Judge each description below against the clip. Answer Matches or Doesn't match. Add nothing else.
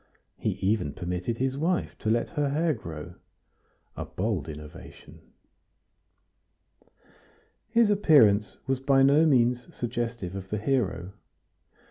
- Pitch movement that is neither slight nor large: Doesn't match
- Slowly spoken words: Matches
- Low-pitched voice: Matches